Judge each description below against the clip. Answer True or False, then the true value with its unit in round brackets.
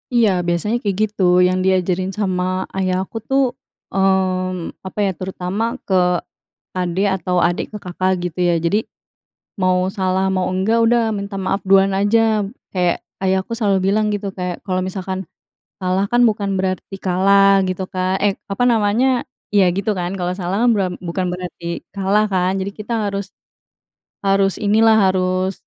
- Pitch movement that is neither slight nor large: False (1.8 semitones)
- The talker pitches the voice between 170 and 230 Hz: True (190 Hz)